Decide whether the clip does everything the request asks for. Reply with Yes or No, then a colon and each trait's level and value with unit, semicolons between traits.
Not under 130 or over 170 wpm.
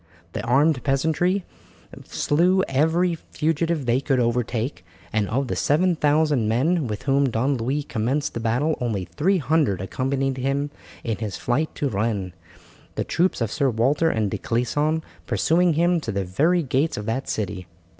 Yes: average, 155 wpm